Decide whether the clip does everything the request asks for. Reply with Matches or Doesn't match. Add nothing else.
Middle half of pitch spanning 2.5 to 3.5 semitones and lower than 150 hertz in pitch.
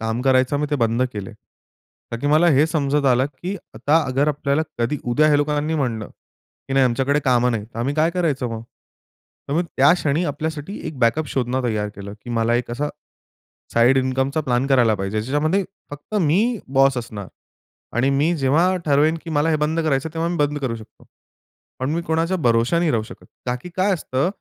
Doesn't match